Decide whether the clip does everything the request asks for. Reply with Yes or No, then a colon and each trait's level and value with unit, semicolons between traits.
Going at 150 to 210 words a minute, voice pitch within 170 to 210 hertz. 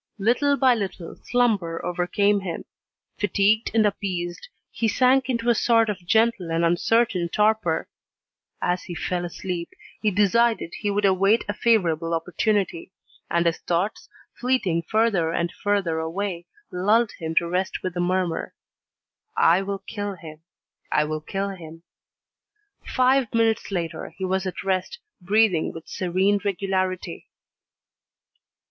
No: slow, 135 wpm; high, 190 Hz